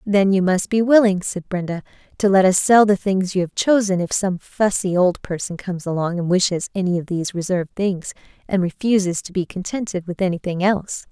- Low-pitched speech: No, medium, 185 Hz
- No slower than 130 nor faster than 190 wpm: No, fast, 205 wpm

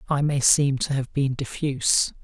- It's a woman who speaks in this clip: No, male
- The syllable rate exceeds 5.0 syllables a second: No, 4.6 syllables/s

